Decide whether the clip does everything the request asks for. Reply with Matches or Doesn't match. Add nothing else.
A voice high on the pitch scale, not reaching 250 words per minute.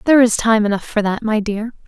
Doesn't match